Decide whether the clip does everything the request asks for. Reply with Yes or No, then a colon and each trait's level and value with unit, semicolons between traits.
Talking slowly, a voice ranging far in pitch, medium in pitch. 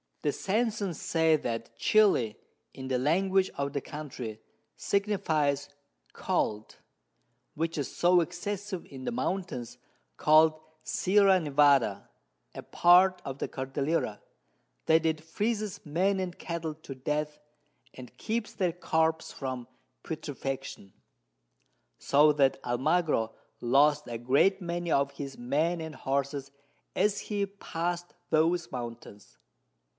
No: slow, 120 wpm; average, 4.7 semitones; medium, 155 Hz